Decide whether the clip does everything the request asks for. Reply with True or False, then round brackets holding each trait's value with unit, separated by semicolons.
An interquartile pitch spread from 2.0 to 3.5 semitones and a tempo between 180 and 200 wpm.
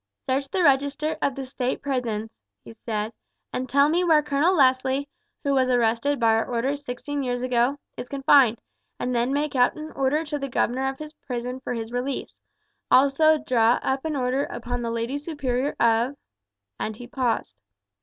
True (2.9 semitones; 185 wpm)